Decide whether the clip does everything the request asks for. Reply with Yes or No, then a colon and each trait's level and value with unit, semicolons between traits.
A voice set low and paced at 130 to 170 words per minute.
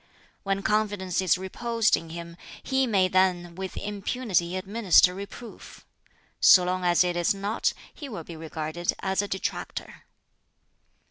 No: high, 190 Hz; average, 140 wpm